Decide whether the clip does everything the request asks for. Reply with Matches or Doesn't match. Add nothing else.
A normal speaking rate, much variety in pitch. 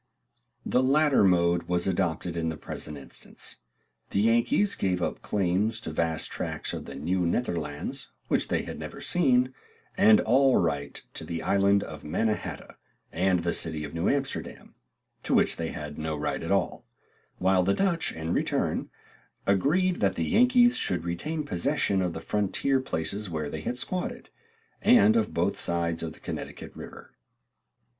Matches